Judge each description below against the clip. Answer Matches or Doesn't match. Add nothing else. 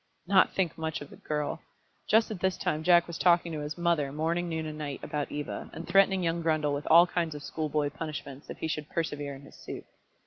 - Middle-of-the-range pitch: Matches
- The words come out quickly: Matches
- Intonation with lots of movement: Doesn't match